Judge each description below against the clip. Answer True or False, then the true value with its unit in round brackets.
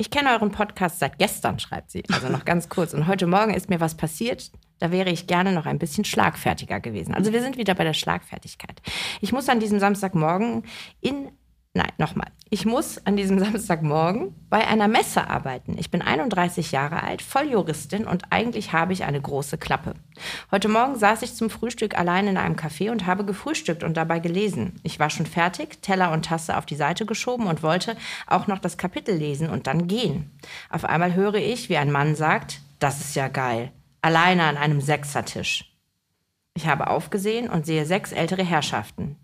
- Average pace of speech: False (195 wpm)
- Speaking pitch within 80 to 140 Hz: False (180 Hz)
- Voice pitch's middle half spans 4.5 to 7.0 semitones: True (4.8 semitones)